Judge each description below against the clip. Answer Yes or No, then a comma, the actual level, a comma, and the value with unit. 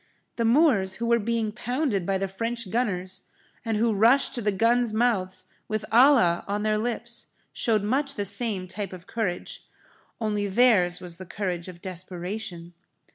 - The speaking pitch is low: No, high, 210 Hz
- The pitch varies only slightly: No, average, 3.9 semitones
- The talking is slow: No, average, 165 wpm